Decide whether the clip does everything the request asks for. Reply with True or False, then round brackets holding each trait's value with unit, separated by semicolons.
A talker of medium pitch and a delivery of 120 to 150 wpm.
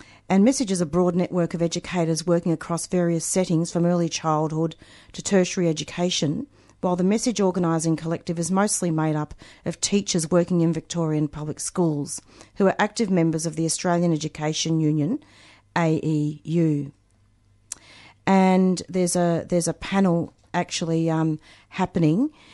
True (170 Hz; 140 wpm)